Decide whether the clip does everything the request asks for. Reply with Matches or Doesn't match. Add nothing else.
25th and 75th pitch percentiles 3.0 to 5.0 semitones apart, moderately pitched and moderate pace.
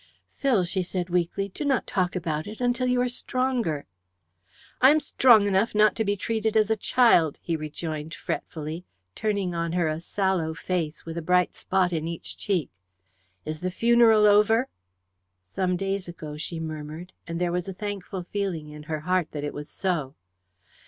Matches